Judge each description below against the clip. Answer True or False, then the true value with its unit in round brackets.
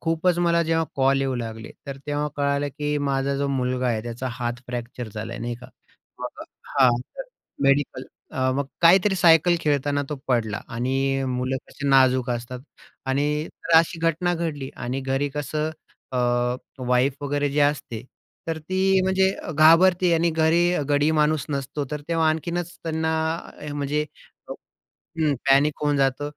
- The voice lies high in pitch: False (145 Hz)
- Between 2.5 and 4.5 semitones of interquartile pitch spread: True (3.6 semitones)